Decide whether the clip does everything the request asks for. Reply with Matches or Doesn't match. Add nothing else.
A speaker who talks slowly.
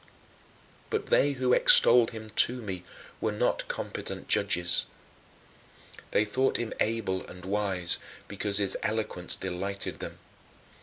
Matches